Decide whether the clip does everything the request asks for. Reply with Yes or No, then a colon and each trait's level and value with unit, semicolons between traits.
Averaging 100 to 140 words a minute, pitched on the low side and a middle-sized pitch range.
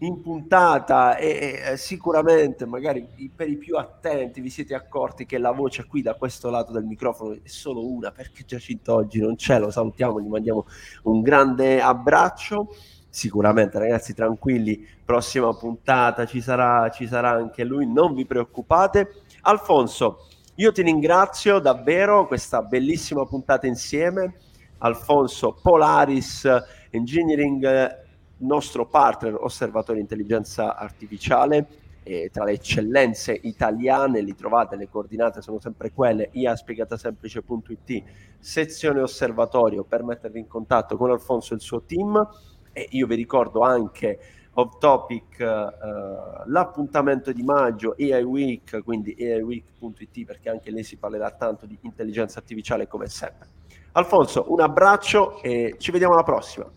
Yes: average, 135 wpm; low, 125 Hz; average, 4.0 semitones